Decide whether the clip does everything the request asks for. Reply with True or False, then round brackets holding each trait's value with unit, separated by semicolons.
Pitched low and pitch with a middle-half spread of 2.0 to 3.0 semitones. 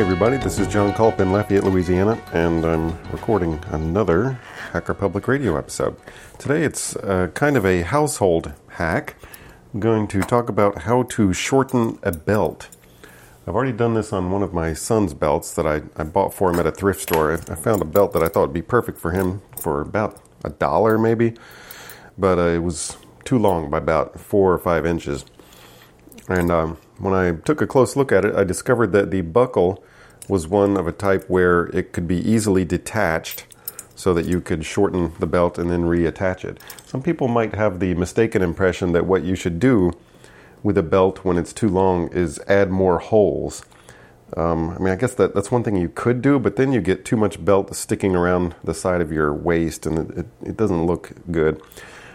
False (95 Hz; 3.8 semitones)